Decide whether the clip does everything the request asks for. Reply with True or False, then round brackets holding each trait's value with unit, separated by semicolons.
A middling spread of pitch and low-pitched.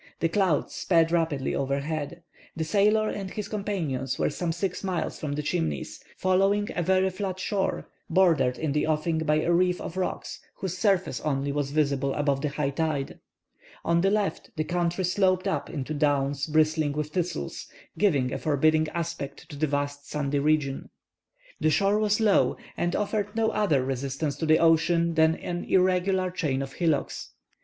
False (4.5 semitones; 160 Hz)